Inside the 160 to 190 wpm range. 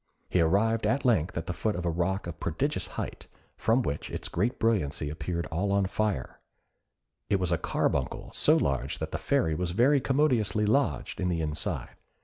Yes: average, 185 wpm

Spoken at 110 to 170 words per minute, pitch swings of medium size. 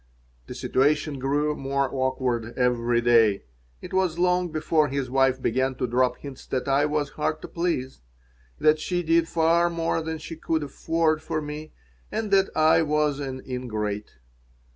Yes: average, 165 wpm; average, 3.7 semitones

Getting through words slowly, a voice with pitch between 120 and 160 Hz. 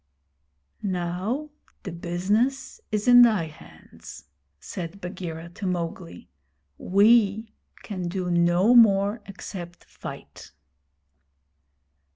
No: slow, 90 wpm; high, 190 Hz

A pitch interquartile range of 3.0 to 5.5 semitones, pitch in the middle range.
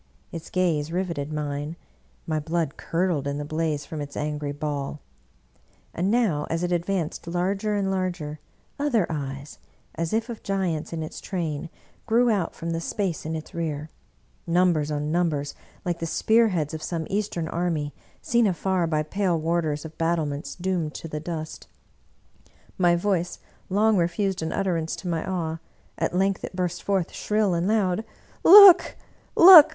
Yes: average, 3.7 semitones; medium, 170 Hz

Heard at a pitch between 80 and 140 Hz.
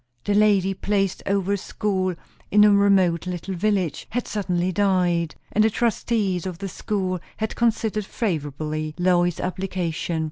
No: high, 190 Hz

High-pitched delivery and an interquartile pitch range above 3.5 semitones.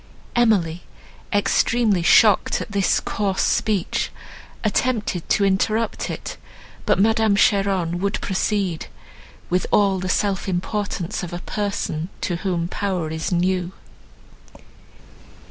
No: high, 195 Hz; average, 2.8 semitones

